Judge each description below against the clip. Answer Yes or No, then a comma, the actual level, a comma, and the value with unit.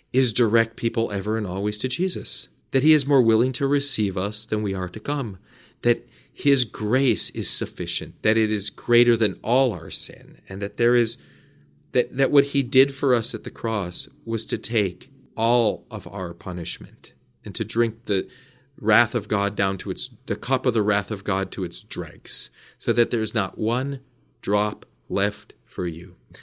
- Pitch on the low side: Yes, low, 115 Hz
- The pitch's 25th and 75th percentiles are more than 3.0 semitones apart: Yes, average, 3.7 semitones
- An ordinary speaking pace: Yes, average, 195 wpm